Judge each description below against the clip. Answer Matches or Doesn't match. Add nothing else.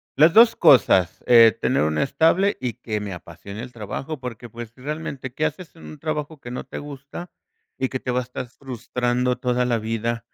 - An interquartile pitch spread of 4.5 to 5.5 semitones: Doesn't match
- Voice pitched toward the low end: Matches